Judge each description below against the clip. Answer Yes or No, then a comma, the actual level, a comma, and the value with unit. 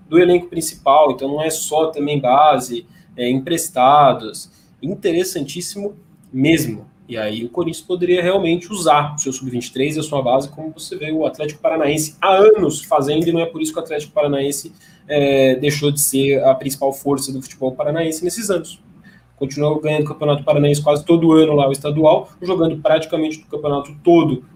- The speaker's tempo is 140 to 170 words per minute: No, average, 180 wpm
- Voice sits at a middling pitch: Yes, medium, 155 Hz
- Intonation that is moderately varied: Yes, average, 3.1 semitones